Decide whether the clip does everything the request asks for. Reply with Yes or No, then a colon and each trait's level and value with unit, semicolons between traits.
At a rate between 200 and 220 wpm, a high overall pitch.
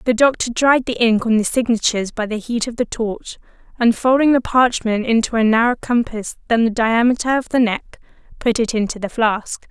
Yes: fast, 205 wpm; high, 230 Hz